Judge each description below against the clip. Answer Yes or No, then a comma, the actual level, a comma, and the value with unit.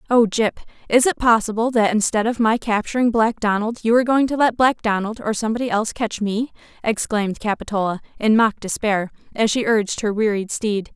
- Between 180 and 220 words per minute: Yes, average, 190 wpm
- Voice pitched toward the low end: No, high, 220 Hz